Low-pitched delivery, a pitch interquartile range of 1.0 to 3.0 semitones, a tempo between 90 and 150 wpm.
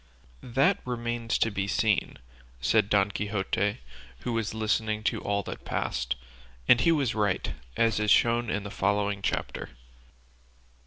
Yes: low, 105 Hz; narrow, 2.5 semitones; average, 145 wpm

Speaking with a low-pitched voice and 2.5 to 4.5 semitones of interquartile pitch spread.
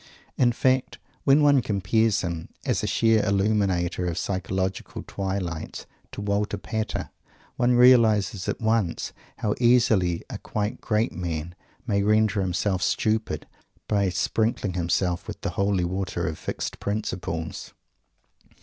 Yes: low, 100 Hz; average, 3.3 semitones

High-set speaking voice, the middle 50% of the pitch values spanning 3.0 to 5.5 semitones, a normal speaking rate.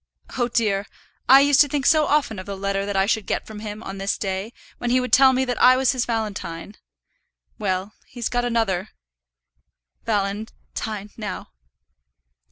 Yes: high, 220 Hz; average, 4.1 semitones; average, 175 wpm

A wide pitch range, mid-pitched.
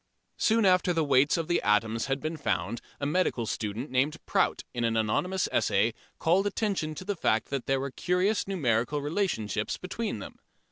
Yes: wide, 7.7 semitones; medium, 145 Hz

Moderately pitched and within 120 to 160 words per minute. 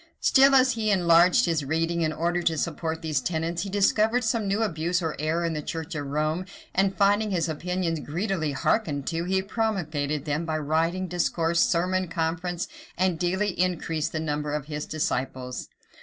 No: medium, 170 Hz; average, 180 wpm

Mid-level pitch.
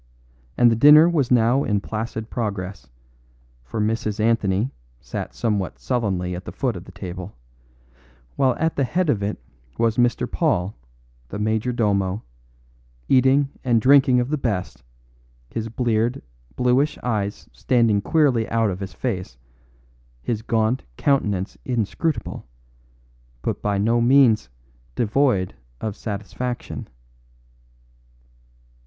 No: low, 115 Hz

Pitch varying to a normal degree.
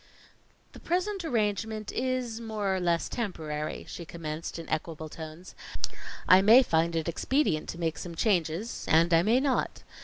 No: wide, 5.8 semitones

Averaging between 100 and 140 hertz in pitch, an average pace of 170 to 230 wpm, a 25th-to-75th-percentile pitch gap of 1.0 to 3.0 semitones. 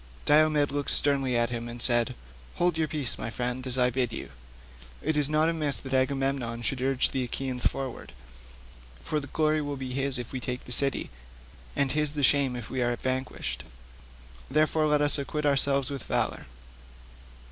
Yes: low, 135 Hz; average, 180 wpm; average, 2.7 semitones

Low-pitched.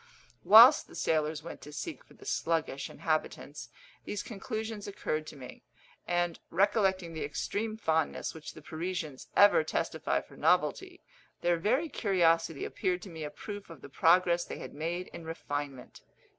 No: medium, 170 Hz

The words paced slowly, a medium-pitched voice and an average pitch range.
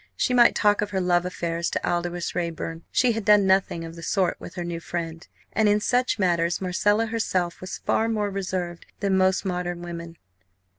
No: average, 195 wpm; medium, 180 Hz; average, 3.2 semitones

